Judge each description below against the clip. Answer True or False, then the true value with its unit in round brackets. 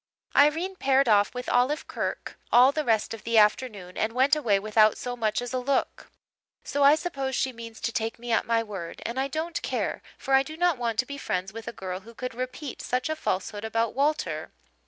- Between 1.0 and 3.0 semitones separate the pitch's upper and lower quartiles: False (3.8 semitones)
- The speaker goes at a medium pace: False (220 wpm)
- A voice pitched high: True (245 Hz)